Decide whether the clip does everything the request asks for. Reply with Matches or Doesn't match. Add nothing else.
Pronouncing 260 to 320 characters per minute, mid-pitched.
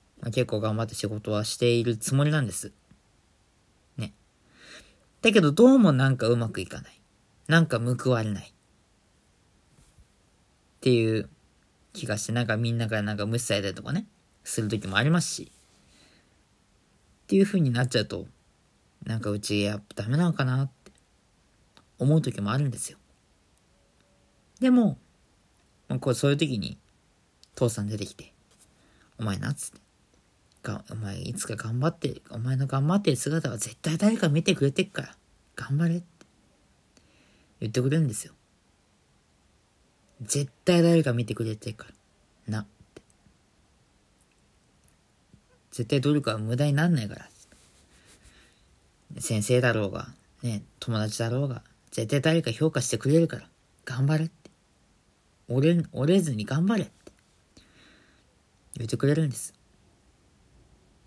Doesn't match